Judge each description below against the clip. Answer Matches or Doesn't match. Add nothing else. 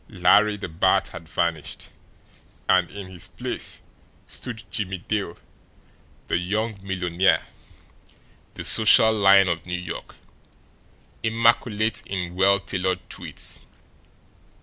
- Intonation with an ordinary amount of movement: Matches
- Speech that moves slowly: Matches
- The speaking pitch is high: Doesn't match